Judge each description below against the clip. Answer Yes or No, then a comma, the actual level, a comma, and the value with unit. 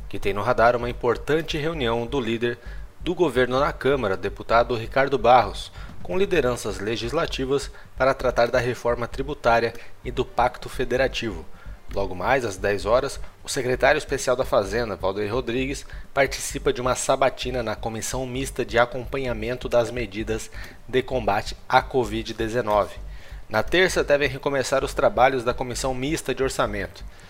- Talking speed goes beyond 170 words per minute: No, average, 145 wpm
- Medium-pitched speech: No, low, 120 Hz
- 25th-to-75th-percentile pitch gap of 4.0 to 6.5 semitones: No, average, 3.0 semitones